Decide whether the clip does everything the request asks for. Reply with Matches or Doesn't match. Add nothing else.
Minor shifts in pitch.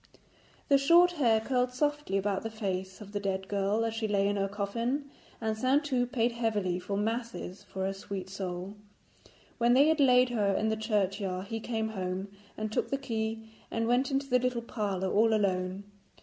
Doesn't match